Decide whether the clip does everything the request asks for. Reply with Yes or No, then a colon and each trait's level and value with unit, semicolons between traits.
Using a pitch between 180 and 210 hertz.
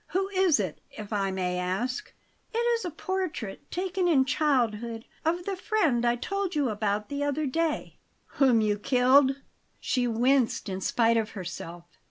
No: very high, 255 Hz